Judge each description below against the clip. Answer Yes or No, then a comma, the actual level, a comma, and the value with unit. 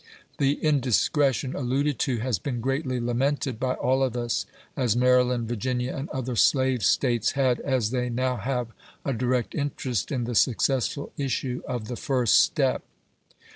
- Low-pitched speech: Yes, low, 125 Hz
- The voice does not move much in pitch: Yes, narrow, 1.9 semitones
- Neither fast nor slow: Yes, average, 155 wpm